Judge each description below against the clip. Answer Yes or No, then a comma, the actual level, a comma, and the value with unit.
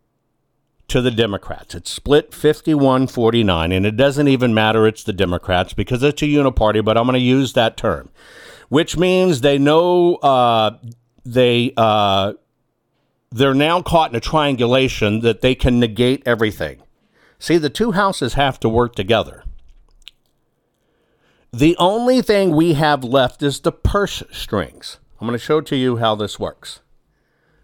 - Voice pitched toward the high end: No, low, 130 Hz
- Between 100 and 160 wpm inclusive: Yes, average, 150 wpm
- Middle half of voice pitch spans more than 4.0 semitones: Yes, average, 4.6 semitones